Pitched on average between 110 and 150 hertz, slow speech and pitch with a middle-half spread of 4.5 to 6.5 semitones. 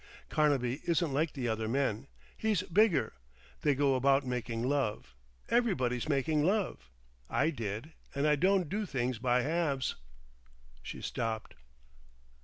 Yes: medium, 140 Hz; slow, 130 wpm; average, 4.8 semitones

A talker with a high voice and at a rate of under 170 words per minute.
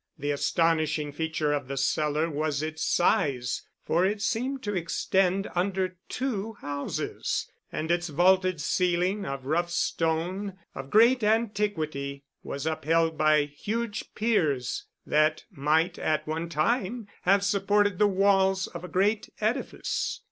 No: medium, 175 Hz; slow, 135 wpm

